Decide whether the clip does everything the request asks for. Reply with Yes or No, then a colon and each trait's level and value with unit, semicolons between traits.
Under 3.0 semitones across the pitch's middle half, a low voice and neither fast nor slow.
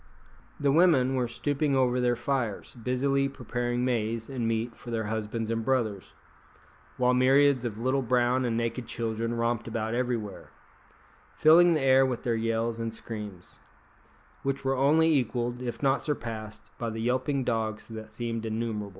Yes: narrow, 2.6 semitones; low, 120 Hz; average, 160 wpm